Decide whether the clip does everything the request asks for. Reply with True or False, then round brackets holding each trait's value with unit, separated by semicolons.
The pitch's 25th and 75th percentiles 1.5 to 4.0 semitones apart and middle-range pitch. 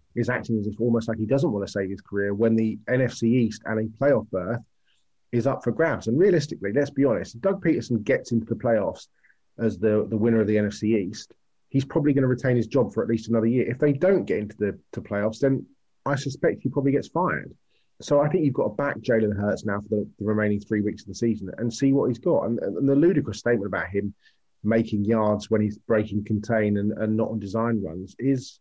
False (3.4 semitones; 115 Hz)